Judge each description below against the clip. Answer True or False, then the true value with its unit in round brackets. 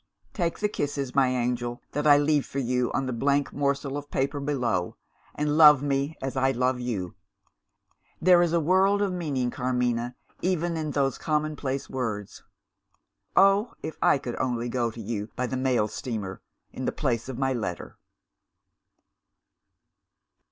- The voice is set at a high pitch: False (135 Hz)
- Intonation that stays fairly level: False (3.4 semitones)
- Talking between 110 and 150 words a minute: False (160 wpm)